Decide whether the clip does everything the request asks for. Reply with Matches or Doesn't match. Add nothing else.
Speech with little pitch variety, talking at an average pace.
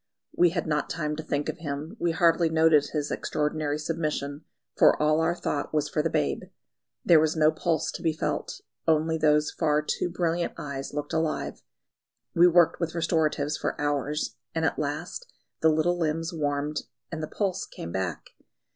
Matches